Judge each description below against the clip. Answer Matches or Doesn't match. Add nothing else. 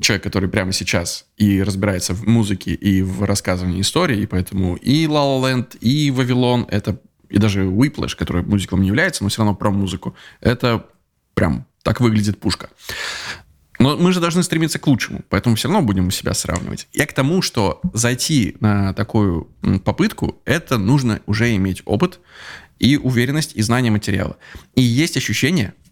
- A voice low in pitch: Matches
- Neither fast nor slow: Doesn't match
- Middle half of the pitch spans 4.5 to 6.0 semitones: Matches